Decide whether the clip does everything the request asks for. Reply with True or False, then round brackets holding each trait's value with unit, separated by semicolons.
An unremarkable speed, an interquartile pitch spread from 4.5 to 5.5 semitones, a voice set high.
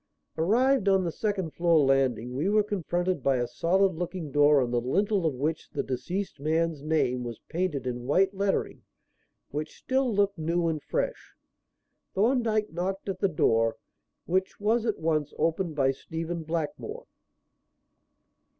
False (150 wpm; 5.2 semitones; 165 Hz)